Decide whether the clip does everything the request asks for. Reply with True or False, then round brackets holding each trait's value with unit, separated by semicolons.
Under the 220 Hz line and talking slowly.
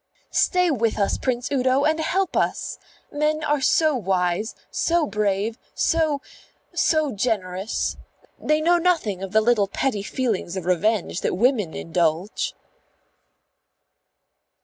False (235 Hz; 125 wpm)